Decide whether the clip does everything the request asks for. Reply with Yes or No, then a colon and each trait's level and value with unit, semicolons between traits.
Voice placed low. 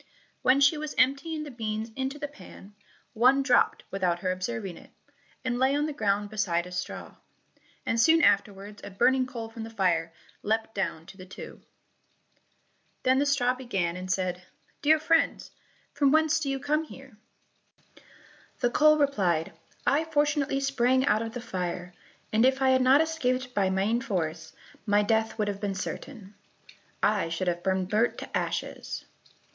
No: high, 230 Hz